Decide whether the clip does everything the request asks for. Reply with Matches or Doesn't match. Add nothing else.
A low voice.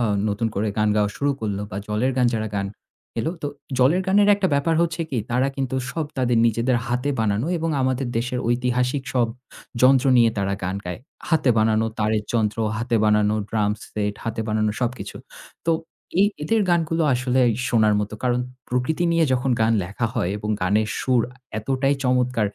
Matches